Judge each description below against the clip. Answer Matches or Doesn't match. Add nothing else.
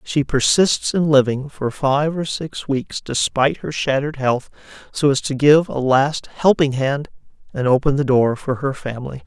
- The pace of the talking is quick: Doesn't match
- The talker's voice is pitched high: Doesn't match